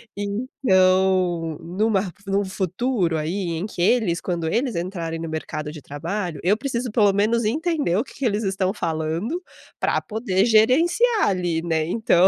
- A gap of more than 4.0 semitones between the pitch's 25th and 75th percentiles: Yes, average, 4.8 semitones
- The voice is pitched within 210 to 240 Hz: No, high, 190 Hz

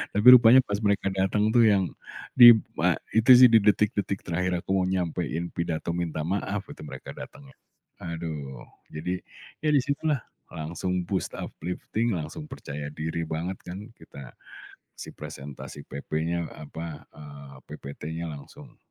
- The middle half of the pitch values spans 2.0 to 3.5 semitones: No, average, 4.8 semitones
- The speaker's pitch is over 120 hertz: No, very low, 90 Hz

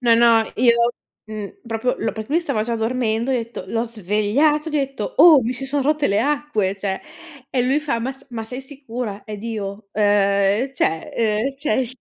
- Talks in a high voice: Yes, high, 230 Hz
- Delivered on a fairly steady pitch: No, average, 4.0 semitones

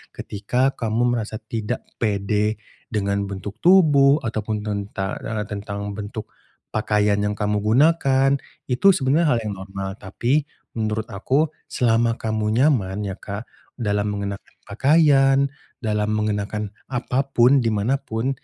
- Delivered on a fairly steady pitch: No, average, 3.6 semitones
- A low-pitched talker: Yes, low, 110 Hz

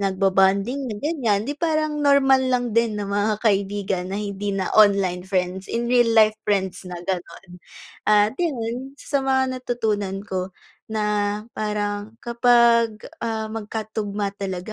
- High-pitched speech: Yes, high, 210 Hz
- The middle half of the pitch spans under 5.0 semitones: Yes, average, 3.4 semitones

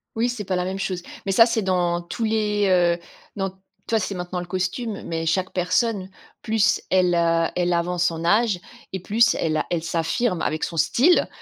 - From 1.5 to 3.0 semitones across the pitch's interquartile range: No, average, 3.5 semitones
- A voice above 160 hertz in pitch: Yes, medium, 185 Hz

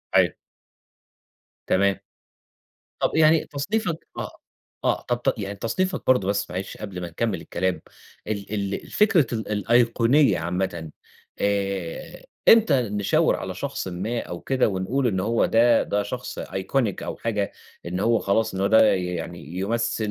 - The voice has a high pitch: No, low, 105 Hz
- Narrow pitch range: No, average, 4.3 semitones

